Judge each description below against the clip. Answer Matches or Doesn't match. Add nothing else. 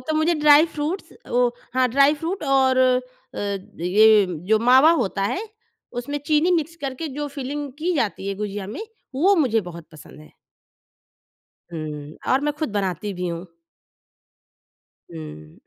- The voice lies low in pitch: Doesn't match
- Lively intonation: Matches